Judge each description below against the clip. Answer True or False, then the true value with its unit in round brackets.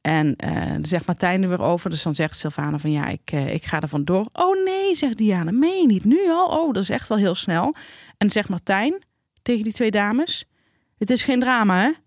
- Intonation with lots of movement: True (8.2 semitones)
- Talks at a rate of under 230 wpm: False (240 wpm)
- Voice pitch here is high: True (205 Hz)